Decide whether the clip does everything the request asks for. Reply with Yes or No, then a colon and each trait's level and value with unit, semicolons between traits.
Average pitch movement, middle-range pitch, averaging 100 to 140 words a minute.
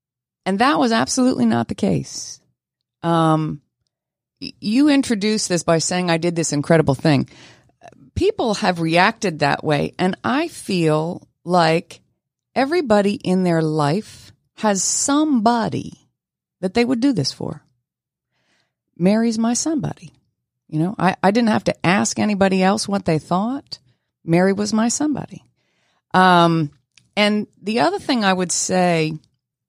No: wide, 6.2 semitones; medium, 180 Hz; slow, 135 wpm